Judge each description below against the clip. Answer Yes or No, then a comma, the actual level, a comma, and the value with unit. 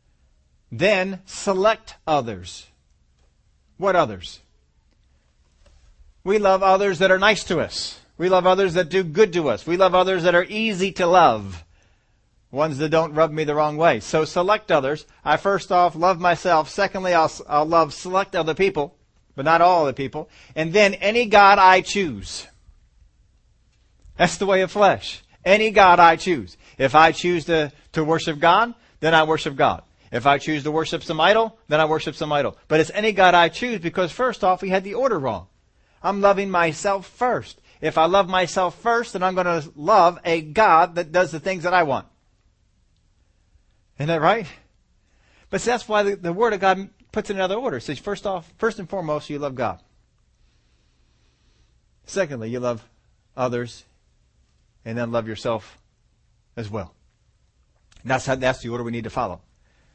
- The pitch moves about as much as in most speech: No, wide, 8.4 semitones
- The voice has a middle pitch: Yes, medium, 160 Hz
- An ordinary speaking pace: Yes, average, 180 wpm